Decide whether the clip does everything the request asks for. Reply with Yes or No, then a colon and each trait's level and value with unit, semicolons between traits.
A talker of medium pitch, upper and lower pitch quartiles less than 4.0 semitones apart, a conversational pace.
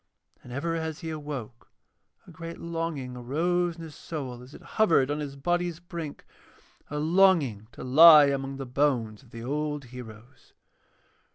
No: medium, 150 Hz; average, 4.6 semitones; average, 160 wpm